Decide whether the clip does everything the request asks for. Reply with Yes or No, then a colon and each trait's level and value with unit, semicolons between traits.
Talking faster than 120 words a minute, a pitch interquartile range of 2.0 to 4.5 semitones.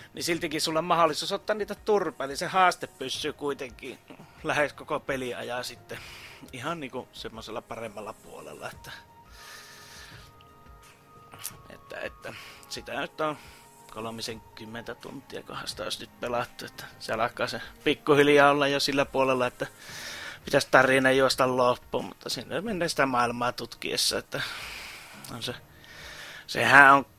Yes: average, 130 wpm; average, 4.0 semitones